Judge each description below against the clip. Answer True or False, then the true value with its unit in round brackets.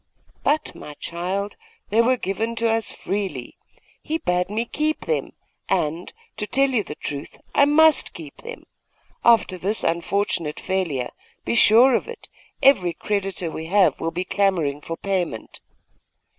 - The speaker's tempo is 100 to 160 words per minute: True (155 wpm)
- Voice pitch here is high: True (195 Hz)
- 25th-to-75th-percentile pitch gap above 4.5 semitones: True (5.5 semitones)